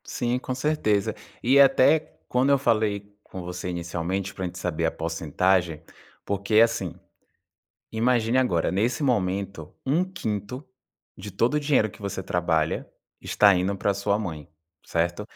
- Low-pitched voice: Yes, low, 100 Hz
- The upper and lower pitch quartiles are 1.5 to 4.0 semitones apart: No, wide, 5.4 semitones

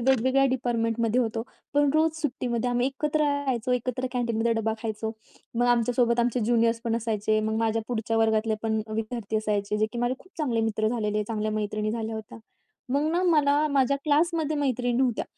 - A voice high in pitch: Yes, high, 235 Hz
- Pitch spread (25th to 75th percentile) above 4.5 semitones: No, average, 3.0 semitones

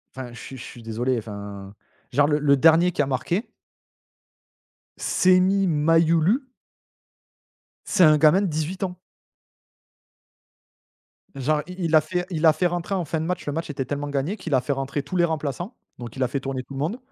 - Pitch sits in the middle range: Yes, medium, 155 Hz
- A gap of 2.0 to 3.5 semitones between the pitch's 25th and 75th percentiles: No, average, 4.5 semitones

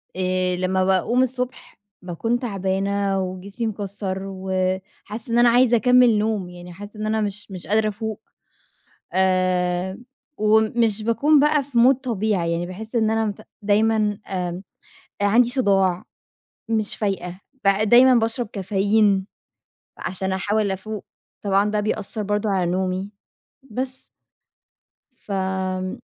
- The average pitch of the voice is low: No, high, 205 Hz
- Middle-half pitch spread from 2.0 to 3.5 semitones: Yes, average, 2.9 semitones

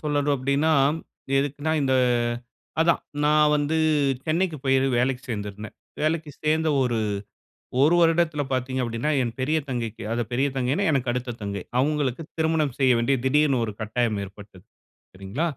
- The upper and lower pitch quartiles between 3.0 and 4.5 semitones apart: Yes, average, 4.2 semitones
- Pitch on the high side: No, low, 135 Hz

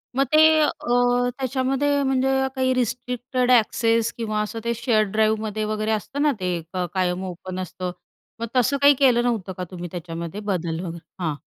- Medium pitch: No, high, 225 Hz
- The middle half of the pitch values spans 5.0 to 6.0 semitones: Yes, wide, 5.4 semitones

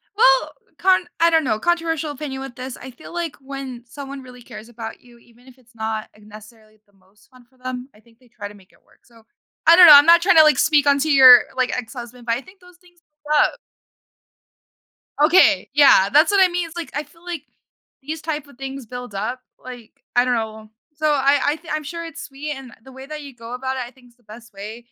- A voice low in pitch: No, very high, 265 Hz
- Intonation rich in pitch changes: No, average, 4.4 semitones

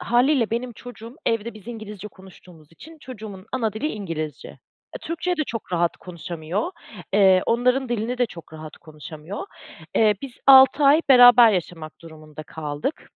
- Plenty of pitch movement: Yes, wide, 6.6 semitones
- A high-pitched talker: Yes, high, 215 Hz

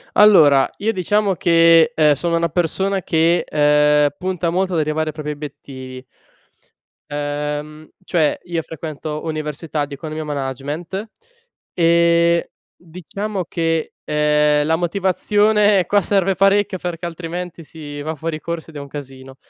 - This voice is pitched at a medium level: Yes, medium, 165 Hz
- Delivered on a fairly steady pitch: No, average, 3.1 semitones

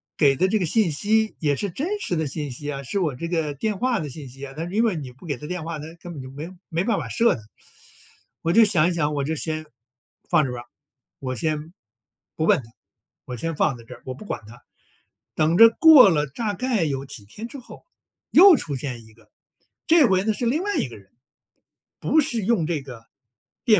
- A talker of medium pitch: Yes, medium, 160 Hz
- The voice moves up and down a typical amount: No, wide, 7.4 semitones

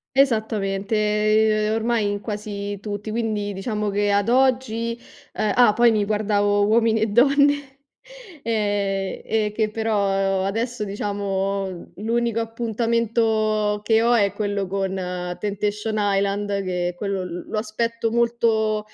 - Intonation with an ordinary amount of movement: No, narrow, 2.0 semitones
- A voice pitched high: Yes, high, 215 Hz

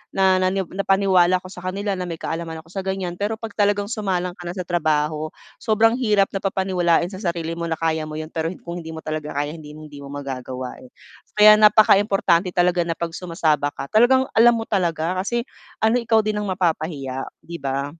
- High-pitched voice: No, medium, 175 Hz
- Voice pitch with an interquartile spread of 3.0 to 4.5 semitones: Yes, average, 3.9 semitones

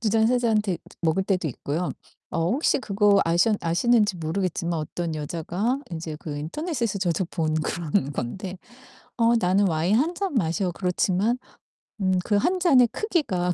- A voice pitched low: No, high, 190 Hz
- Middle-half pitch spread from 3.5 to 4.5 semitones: No, average, 5.3 semitones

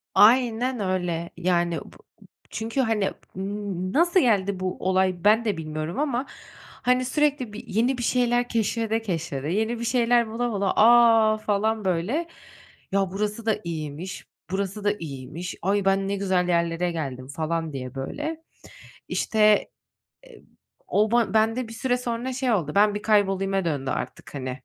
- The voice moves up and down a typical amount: Yes, average, 4.9 semitones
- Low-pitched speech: No, high, 205 Hz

